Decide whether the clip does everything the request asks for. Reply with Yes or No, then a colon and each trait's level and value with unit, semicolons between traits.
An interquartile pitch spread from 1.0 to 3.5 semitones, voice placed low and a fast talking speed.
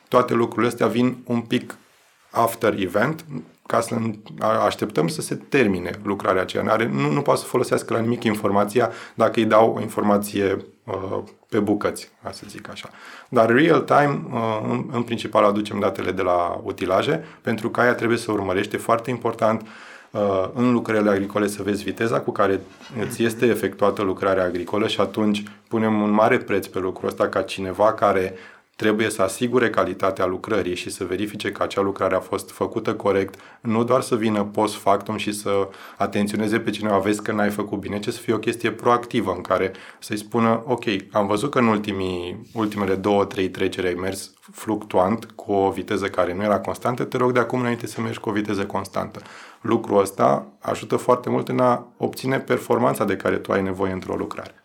Yes: average, 2.8 semitones; low, 105 Hz; fast, 185 wpm